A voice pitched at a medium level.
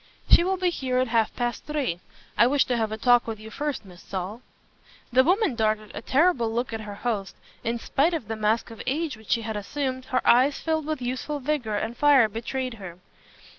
No: high, 240 Hz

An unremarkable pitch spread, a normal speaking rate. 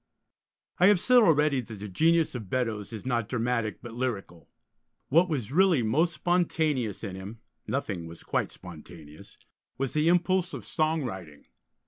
No: wide, 7.7 semitones; average, 155 wpm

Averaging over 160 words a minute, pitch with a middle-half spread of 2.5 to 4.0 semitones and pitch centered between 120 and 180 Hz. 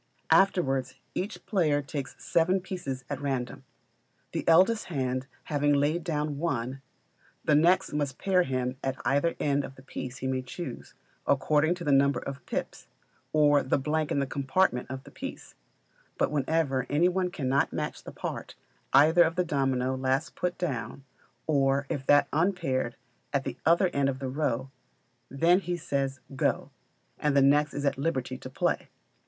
Yes: average, 170 wpm; average, 3.7 semitones; medium, 140 Hz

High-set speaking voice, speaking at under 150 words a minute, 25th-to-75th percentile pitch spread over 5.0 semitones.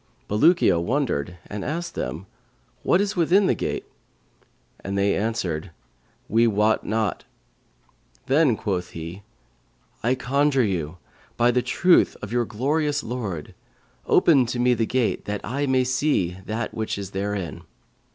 No: low, 115 Hz; average, 140 wpm; wide, 5.6 semitones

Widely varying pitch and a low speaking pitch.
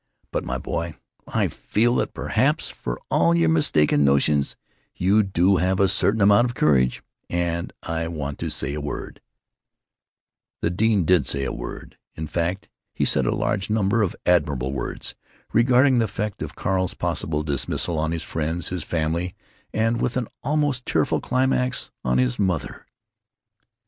Yes: wide, 5.8 semitones; very low, 85 Hz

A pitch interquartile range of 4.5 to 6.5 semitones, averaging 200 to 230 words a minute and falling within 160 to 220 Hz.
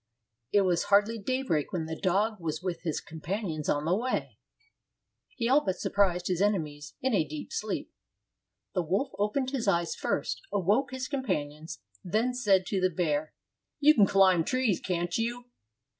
No: wide, 5.5 semitones; average, 170 wpm; high, 190 Hz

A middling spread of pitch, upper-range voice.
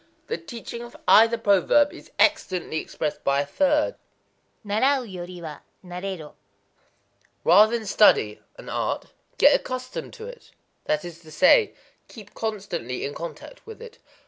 No: wide, 7.7 semitones; high, 210 Hz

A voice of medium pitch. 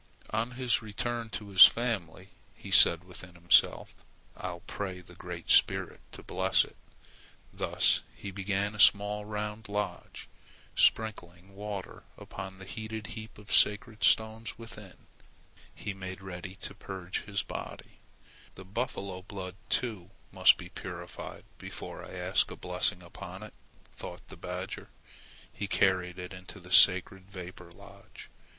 No: very low, 95 Hz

